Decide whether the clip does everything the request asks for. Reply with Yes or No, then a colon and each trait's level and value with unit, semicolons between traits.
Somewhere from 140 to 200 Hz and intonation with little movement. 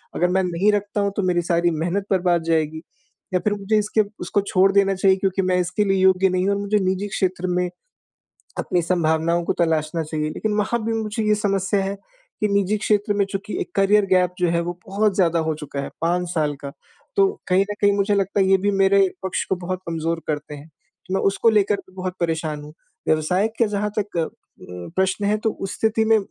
No: high, 190 Hz; average, 3.0 semitones